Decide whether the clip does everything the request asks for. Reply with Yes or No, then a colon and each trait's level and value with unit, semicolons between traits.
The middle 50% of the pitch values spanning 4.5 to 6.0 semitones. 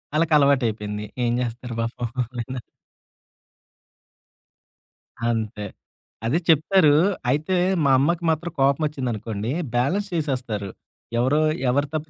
Yes: average, 4.8 semitones